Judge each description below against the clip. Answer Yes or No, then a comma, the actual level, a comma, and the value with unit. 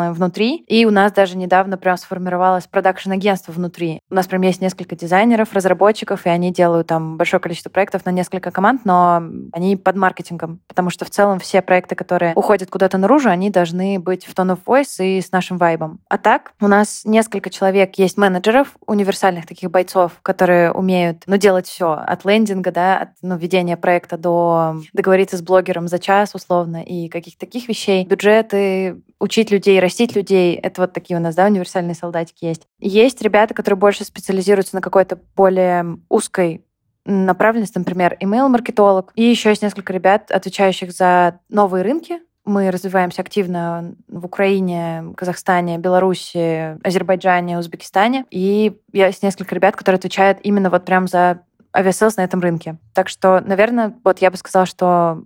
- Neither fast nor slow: No, fast, 165 wpm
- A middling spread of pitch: No, narrow, 2.0 semitones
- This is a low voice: No, medium, 185 Hz